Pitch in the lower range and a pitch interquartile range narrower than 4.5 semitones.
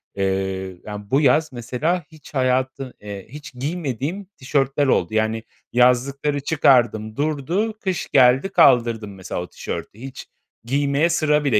No: low, 130 Hz; average, 5.1 semitones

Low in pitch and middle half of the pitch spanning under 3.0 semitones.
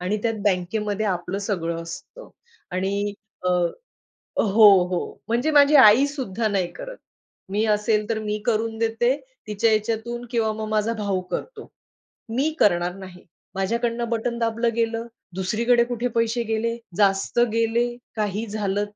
No: high, 220 Hz; narrow, 2.6 semitones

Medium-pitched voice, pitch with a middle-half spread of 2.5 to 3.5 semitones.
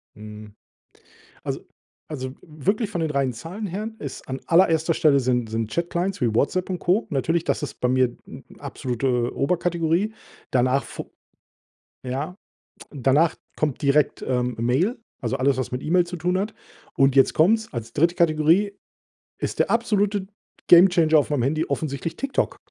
No: medium, 155 Hz; wide, 5.5 semitones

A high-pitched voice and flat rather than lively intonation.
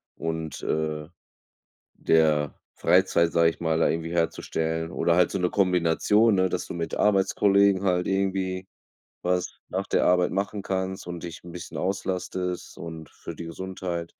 No: very low, 90 Hz; narrow, 2.3 semitones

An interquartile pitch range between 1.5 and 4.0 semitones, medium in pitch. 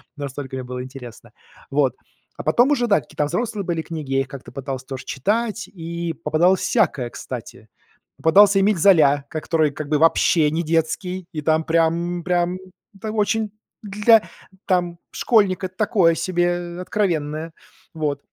No: average, 4.5 semitones; medium, 165 Hz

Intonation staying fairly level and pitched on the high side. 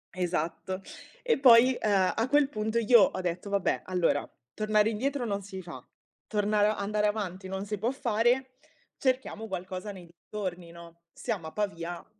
No: average, 3.5 semitones; high, 205 Hz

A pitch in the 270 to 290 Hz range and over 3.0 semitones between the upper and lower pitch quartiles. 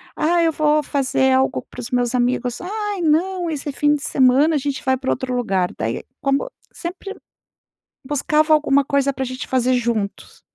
Yes: very high, 275 Hz; average, 3.4 semitones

